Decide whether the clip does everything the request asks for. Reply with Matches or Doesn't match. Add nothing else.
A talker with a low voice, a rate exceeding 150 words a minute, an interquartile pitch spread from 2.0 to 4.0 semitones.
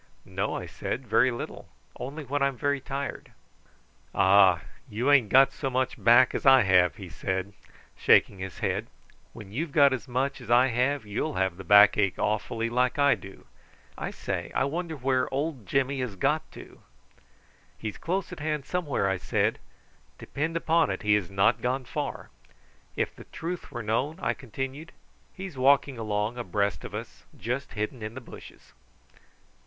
Doesn't match